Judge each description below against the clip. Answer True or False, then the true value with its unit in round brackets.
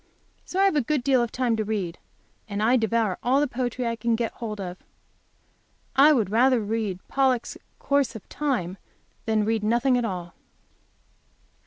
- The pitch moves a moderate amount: True (3.5 semitones)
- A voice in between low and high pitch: False (230 Hz)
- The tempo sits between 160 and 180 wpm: True (175 wpm)